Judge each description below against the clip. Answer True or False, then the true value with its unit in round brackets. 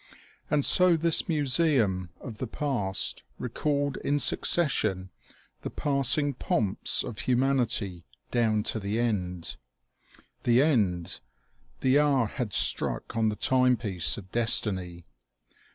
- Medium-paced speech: False (120 wpm)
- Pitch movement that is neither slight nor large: False (5.8 semitones)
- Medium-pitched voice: False (120 Hz)